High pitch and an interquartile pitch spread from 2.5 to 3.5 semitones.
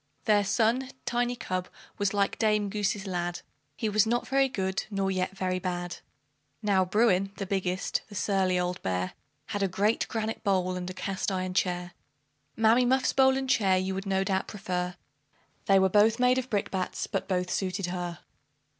Yes: high, 195 Hz; average, 2.8 semitones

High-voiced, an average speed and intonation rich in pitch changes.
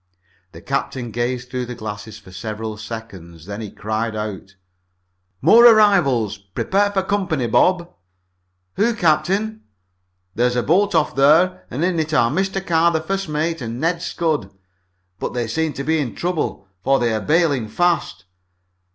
No: medium, 140 Hz; average, 160 wpm; wide, 7.8 semitones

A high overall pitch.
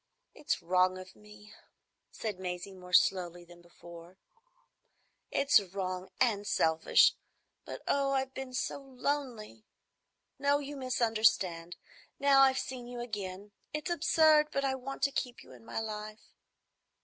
Yes: high, 215 Hz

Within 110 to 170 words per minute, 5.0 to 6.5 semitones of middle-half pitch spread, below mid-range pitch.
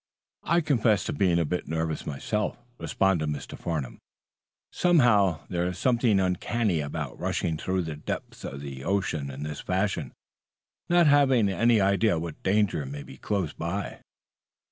Yes: average, 150 wpm; wide, 5.5 semitones; very low, 95 Hz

